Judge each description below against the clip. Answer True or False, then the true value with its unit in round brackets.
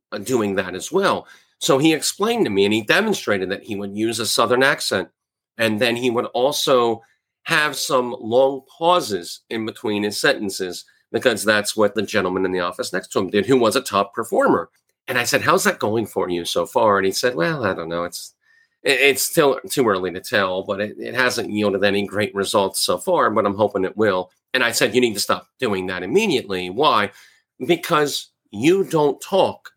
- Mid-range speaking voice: False (105 Hz)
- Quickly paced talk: True (210 wpm)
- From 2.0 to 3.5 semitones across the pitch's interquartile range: False (4.7 semitones)